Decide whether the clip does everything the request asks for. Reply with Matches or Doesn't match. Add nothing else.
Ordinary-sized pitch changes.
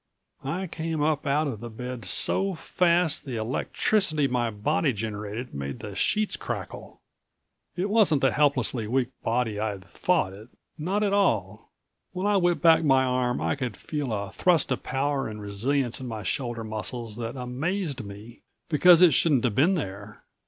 Doesn't match